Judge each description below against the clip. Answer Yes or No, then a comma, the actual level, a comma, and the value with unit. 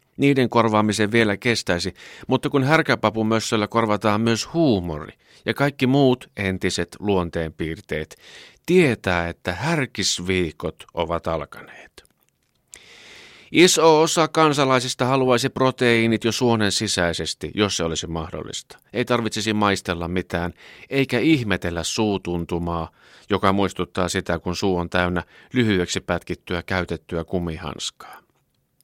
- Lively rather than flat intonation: Yes, wide, 5.7 semitones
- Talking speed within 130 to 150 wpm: No, average, 105 wpm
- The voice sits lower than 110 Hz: Yes, low, 100 Hz